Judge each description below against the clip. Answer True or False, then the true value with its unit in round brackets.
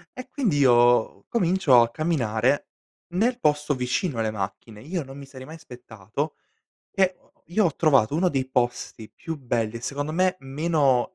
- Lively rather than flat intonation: True (5.7 semitones)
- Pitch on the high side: False (140 Hz)